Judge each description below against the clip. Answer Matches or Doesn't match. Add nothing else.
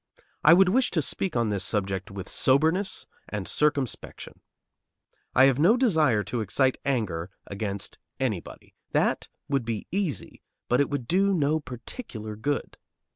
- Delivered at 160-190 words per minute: Doesn't match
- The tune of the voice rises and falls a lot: Matches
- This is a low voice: Matches